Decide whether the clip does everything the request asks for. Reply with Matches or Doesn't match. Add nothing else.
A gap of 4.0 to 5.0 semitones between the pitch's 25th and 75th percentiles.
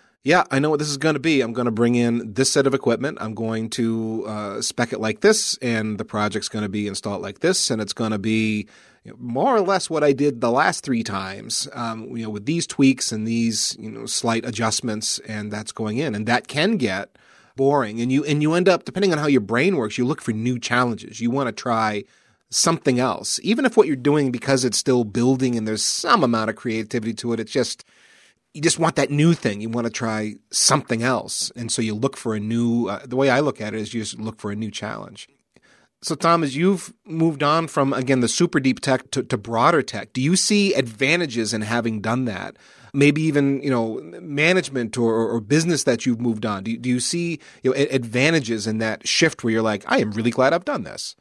Matches